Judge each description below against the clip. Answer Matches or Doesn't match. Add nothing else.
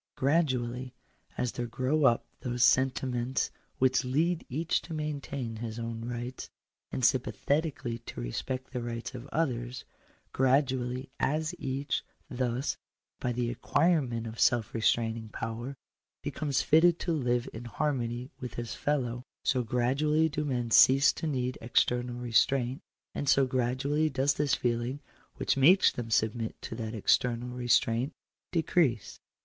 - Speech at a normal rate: Matches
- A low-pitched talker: Matches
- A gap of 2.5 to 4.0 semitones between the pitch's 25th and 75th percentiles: Matches